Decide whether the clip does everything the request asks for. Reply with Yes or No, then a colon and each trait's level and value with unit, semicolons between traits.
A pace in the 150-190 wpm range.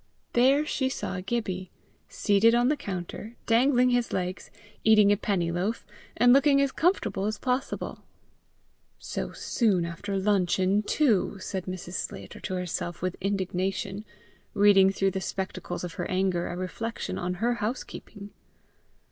No: average, 140 wpm